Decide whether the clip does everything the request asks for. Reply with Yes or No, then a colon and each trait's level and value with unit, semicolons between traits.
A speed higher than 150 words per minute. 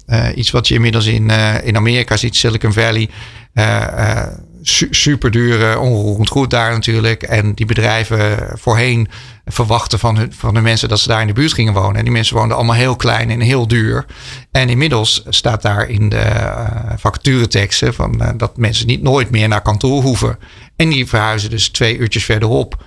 Yes: average, 195 wpm